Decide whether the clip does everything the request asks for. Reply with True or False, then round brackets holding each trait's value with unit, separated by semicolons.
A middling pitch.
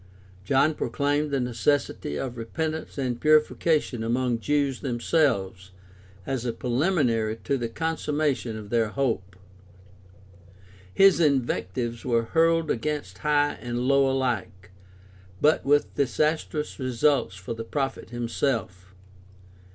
False (130 Hz)